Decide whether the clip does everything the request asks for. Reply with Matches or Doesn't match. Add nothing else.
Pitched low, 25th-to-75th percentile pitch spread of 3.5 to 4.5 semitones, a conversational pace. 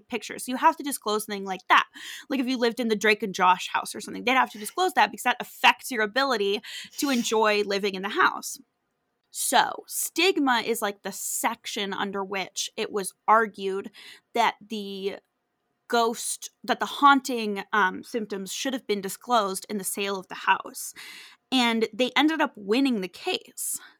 Doesn't match